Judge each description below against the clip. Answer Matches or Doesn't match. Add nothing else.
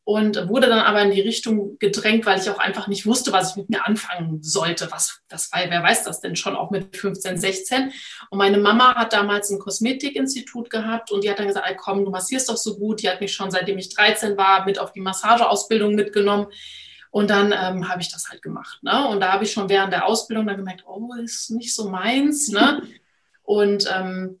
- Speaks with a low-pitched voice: Doesn't match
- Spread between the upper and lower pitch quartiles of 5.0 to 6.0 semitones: Doesn't match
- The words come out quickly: Matches